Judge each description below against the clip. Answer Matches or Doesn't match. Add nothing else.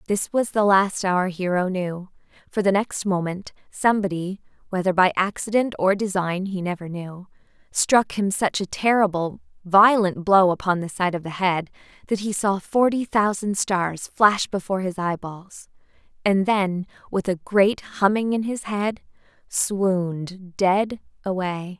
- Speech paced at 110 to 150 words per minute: Matches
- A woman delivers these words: Matches